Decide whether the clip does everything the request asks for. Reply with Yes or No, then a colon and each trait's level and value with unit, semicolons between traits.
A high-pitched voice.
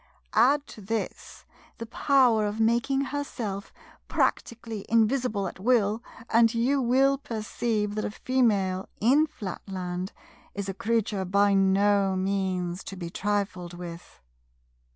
Yes: high, 210 Hz